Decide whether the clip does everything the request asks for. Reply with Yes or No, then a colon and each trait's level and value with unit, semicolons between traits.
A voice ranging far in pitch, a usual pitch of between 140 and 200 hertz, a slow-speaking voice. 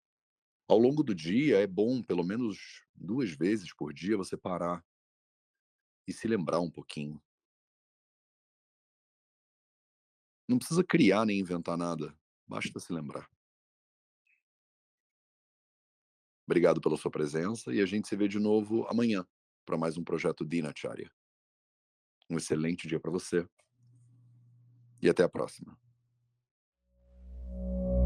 No: wide, 8.0 semitones; very low, 90 Hz; slow, 115 wpm